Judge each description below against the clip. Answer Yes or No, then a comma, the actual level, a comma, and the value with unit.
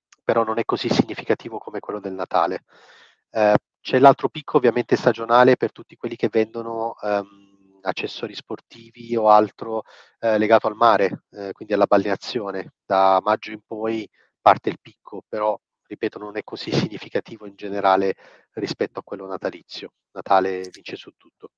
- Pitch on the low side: Yes, low, 105 Hz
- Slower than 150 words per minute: No, average, 155 wpm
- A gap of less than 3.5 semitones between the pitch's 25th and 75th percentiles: Yes, narrow, 2.4 semitones